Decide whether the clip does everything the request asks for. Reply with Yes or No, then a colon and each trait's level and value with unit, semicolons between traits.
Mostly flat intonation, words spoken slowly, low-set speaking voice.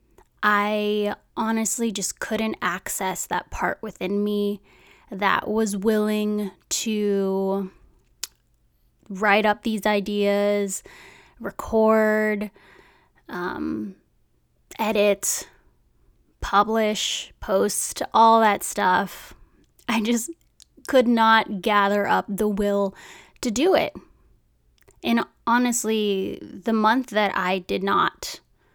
No: narrow, 1.7 semitones; slow, 90 wpm; high, 210 Hz